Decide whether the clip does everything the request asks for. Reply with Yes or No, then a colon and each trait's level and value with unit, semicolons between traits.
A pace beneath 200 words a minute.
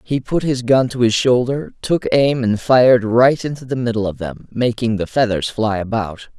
No: fast, 205 wpm